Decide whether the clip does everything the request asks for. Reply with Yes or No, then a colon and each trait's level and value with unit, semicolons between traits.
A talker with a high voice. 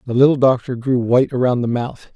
No: low, 125 Hz